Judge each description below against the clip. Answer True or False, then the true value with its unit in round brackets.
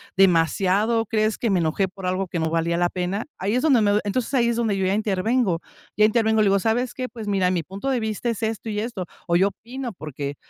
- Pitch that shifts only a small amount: False (3.8 semitones)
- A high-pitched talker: True (205 Hz)